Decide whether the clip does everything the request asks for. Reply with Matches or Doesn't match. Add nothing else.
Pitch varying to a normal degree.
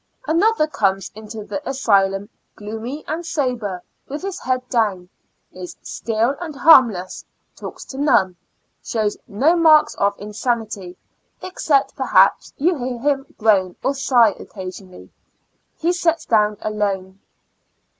Doesn't match